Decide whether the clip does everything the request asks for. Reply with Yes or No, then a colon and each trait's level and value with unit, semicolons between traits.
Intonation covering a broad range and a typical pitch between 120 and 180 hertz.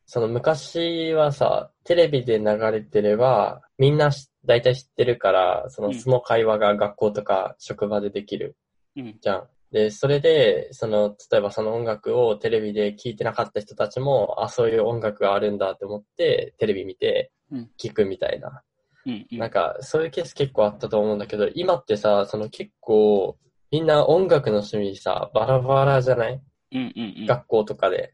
Yes: wide, 8.1 semitones; low, 125 Hz